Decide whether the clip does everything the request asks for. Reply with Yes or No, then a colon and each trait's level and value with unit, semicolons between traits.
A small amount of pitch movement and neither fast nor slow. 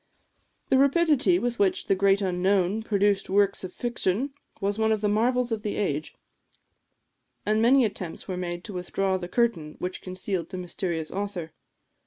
No: average, 3.5 semitones; average, 165 wpm